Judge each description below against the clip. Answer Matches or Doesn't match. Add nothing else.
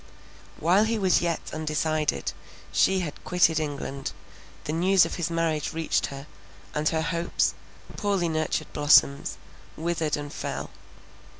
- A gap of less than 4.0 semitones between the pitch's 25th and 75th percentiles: Matches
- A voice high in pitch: Doesn't match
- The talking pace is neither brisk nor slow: Doesn't match